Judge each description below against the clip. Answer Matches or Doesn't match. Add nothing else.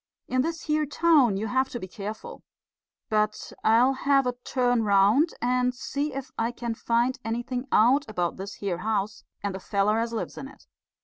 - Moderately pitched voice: Doesn't match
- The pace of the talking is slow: Doesn't match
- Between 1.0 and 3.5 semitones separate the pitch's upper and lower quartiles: Doesn't match